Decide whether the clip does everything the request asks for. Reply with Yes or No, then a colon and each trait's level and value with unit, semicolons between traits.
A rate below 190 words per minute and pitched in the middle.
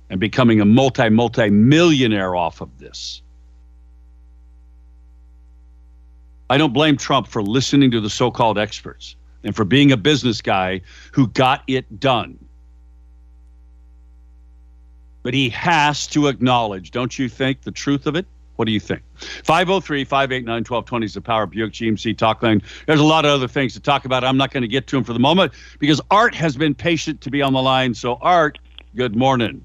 No: average, 180 wpm; low, 115 Hz